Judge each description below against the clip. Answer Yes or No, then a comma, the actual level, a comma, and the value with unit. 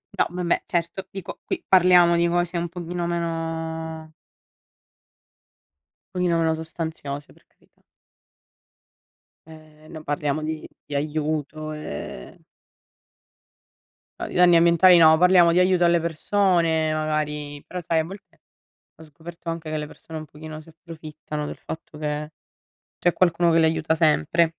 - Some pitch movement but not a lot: No, narrow, 1.8 semitones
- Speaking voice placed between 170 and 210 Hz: No, medium, 160 Hz